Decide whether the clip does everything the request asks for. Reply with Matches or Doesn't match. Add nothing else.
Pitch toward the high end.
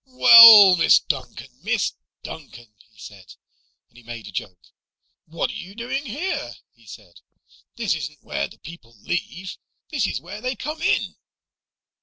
Doesn't match